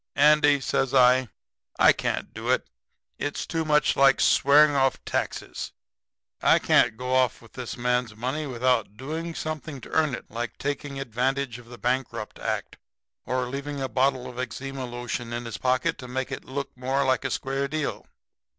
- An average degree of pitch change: No, narrow, 2.2 semitones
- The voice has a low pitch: Yes, low, 130 Hz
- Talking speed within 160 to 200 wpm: Yes, average, 175 wpm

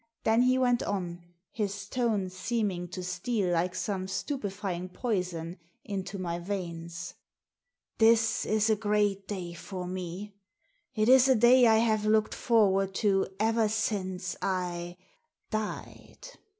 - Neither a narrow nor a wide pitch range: Yes, average, 3.4 semitones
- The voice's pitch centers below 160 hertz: No, high, 200 Hz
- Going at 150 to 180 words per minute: No, slow, 135 wpm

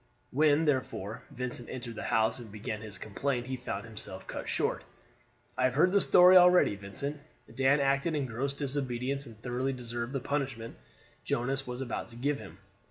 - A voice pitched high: No, low, 130 Hz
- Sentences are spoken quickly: No, average, 175 wpm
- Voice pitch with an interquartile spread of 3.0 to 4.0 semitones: Yes, average, 3.3 semitones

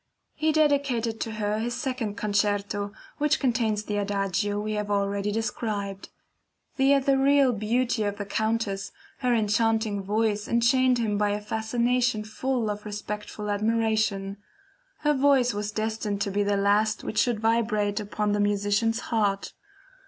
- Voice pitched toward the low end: No, high, 215 Hz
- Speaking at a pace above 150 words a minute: No, average, 145 wpm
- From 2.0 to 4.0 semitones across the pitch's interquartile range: Yes, narrow, 2.4 semitones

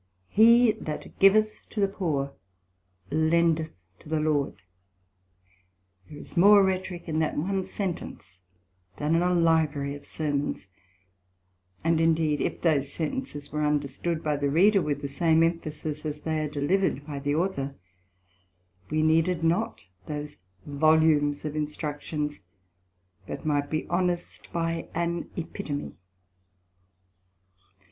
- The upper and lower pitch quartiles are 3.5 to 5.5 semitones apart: No, average, 2.7 semitones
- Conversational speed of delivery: No, slow, 125 wpm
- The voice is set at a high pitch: No, medium, 155 Hz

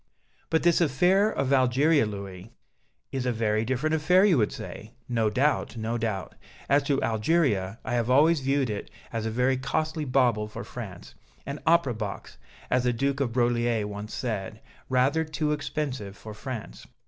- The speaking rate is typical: Yes, average, 170 wpm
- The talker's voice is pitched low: Yes, low, 125 Hz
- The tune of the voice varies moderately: Yes, average, 4.9 semitones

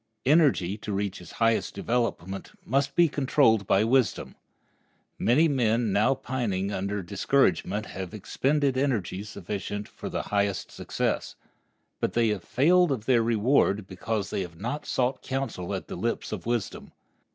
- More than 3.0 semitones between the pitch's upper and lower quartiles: Yes, average, 5.0 semitones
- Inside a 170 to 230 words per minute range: No, average, 150 wpm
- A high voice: No, low, 115 Hz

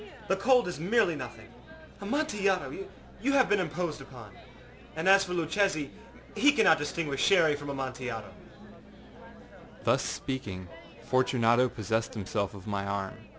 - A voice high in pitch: No, medium, 145 Hz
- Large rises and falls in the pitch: Yes, wide, 8.8 semitones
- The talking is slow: Yes, slow, 130 wpm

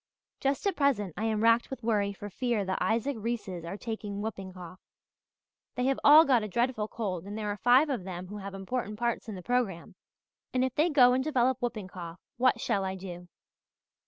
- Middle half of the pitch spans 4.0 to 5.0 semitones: Yes, average, 4.4 semitones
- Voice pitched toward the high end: Yes, high, 220 Hz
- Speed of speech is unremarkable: No, fast, 210 wpm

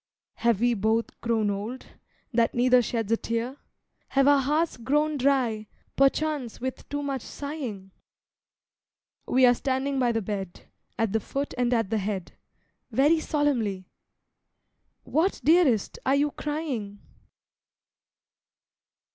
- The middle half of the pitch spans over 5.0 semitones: No, average, 4.2 semitones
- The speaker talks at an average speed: No, slow, 120 wpm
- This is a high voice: Yes, very high, 250 Hz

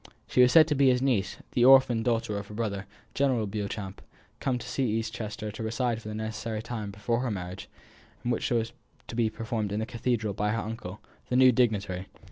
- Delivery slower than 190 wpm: No, fast, 205 wpm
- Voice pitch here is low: Yes, low, 110 Hz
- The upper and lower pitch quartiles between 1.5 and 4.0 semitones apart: Yes, average, 2.8 semitones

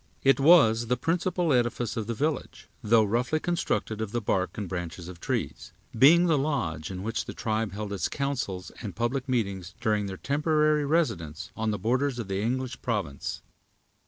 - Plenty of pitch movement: Yes, wide, 5.8 semitones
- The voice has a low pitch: Yes, low, 115 Hz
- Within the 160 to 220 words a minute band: Yes, average, 180 wpm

